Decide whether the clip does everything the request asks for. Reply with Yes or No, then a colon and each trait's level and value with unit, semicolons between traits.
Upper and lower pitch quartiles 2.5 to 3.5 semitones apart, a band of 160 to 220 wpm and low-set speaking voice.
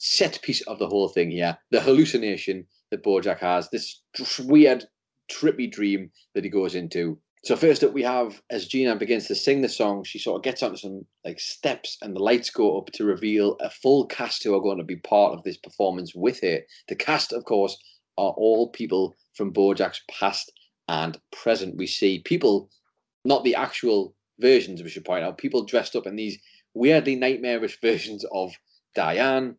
No: average, 4.3 semitones; average, 195 wpm; low, 105 Hz